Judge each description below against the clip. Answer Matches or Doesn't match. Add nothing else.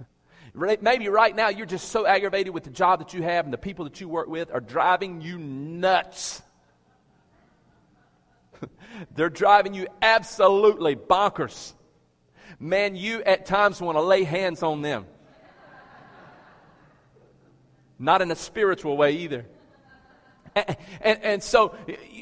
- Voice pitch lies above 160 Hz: Matches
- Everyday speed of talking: Doesn't match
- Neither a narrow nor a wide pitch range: Matches